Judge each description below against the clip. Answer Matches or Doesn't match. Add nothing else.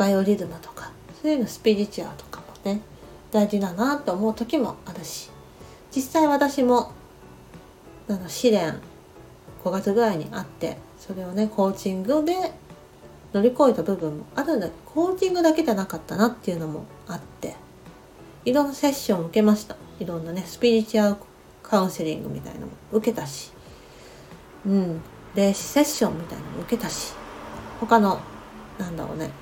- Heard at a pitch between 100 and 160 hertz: Doesn't match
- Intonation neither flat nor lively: Matches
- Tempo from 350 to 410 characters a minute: Matches